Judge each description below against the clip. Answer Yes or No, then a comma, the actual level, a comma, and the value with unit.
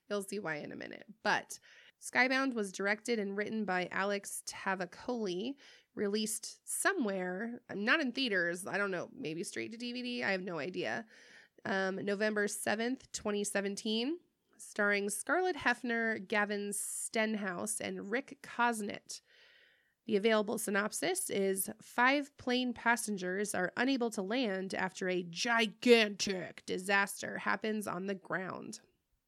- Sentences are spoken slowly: Yes, slow, 130 wpm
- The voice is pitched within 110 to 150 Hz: No, high, 210 Hz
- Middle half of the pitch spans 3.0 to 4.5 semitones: Yes, average, 3.7 semitones